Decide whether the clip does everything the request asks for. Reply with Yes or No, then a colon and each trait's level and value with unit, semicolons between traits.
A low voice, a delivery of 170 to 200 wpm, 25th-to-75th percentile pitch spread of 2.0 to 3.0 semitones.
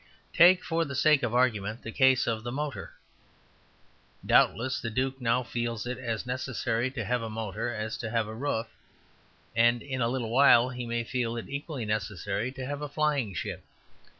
Yes: low, 120 Hz; average, 185 wpm; average, 2.7 semitones